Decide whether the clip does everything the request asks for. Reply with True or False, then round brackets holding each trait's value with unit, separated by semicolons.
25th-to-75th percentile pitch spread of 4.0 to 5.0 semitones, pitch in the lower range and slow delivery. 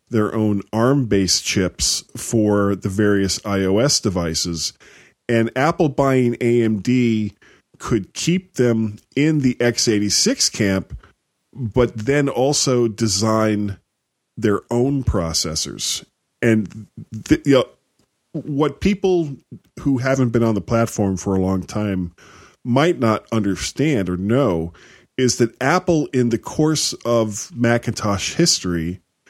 True (4.3 semitones; 115 Hz; 120 wpm)